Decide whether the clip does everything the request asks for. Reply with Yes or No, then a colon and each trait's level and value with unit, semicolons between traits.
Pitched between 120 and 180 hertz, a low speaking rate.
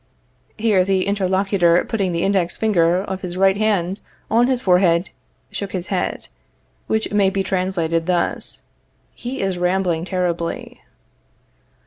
No: high, 190 Hz; slow, 130 wpm